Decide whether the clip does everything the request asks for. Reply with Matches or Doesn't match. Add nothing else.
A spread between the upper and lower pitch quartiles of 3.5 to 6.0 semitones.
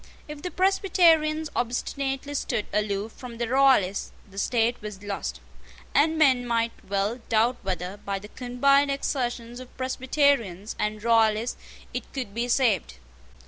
Matches